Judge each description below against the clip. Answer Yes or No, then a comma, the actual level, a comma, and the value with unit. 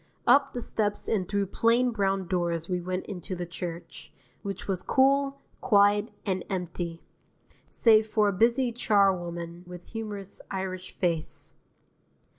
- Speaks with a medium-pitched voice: No, high, 195 Hz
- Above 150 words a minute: No, slow, 135 wpm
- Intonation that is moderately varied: Yes, average, 3.7 semitones